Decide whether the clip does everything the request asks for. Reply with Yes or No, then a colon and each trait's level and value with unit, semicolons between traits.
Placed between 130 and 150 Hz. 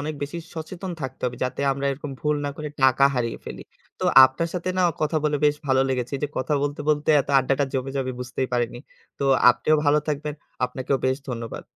Yes: medium, 140 Hz